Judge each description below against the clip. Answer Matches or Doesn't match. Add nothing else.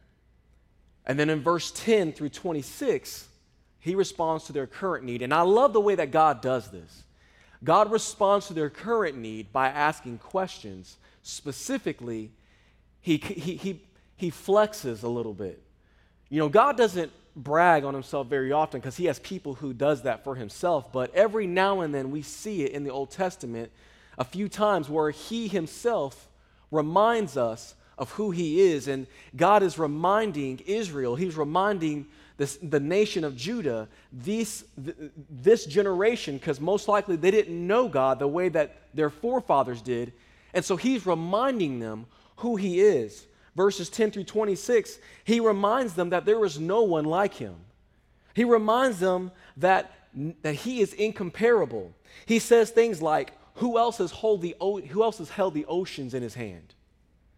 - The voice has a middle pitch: Matches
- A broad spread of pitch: Matches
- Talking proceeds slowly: Doesn't match